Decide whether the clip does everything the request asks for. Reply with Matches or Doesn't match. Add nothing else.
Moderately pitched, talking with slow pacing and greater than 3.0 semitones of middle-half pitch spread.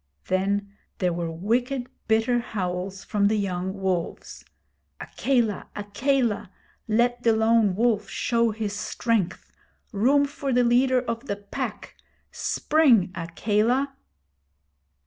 Doesn't match